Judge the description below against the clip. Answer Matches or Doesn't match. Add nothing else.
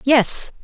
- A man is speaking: Doesn't match